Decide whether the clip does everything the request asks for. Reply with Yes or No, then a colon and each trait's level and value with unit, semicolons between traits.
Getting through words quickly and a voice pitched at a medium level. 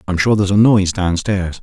No: fast, 220 wpm; very low, 95 Hz